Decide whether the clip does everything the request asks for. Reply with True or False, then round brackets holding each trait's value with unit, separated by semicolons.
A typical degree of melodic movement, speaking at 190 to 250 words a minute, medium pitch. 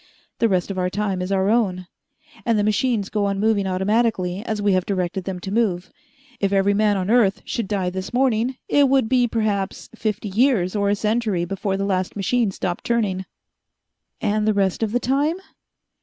False (3.1 semitones; 195 wpm; 205 Hz)